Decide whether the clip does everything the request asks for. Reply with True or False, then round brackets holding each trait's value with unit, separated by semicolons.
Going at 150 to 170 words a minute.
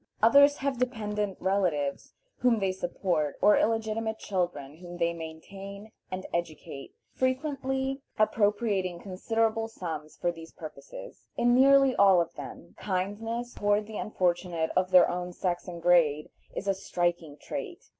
False (135 wpm)